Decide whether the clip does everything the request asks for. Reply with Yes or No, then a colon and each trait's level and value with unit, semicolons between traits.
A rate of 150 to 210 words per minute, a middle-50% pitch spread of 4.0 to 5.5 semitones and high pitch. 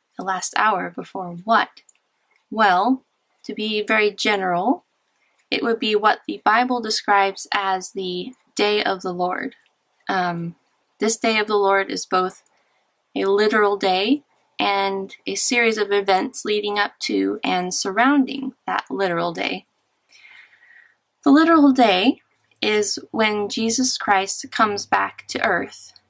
No: slow, 135 wpm; average, 4.3 semitones; high, 210 Hz